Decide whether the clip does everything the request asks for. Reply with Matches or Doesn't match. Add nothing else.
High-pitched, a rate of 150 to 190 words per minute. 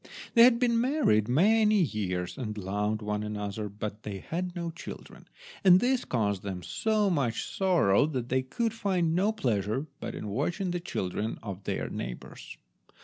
Doesn't match